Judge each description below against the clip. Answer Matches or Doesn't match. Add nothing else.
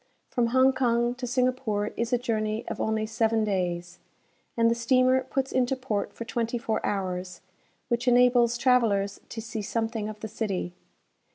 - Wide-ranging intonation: Doesn't match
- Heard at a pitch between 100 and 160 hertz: Doesn't match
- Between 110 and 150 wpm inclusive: Doesn't match